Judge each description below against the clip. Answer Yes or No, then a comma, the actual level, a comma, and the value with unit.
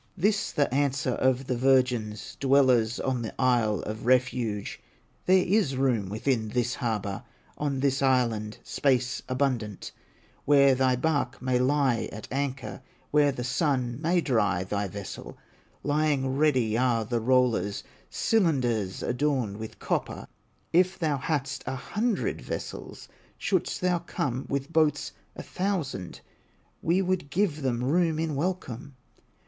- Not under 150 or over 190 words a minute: No, slow, 135 wpm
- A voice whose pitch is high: No, low, 130 Hz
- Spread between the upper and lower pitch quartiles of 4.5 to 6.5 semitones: No, average, 3.7 semitones